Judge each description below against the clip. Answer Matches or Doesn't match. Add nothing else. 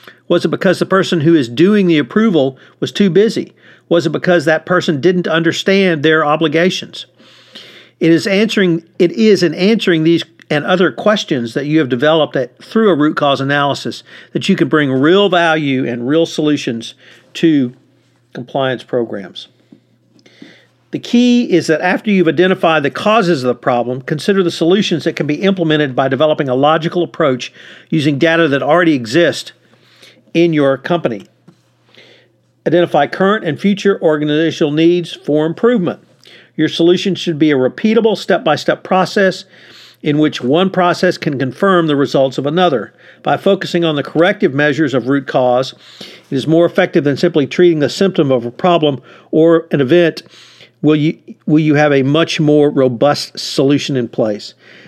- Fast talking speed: Doesn't match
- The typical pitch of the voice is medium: Matches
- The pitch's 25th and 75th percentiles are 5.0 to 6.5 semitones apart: Doesn't match